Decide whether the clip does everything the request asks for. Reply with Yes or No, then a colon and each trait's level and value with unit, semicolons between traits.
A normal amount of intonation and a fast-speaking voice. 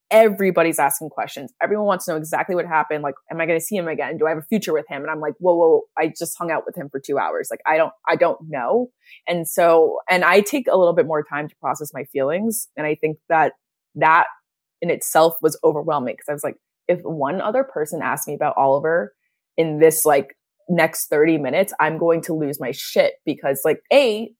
Yes: average, 3.9 semitones; fast, 235 wpm